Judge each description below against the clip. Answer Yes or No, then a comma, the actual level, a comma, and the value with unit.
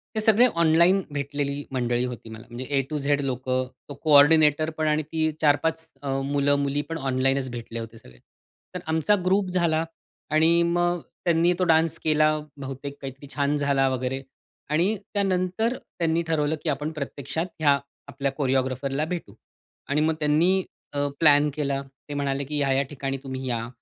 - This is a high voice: No, medium, 145 Hz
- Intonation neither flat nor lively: Yes, average, 3.0 semitones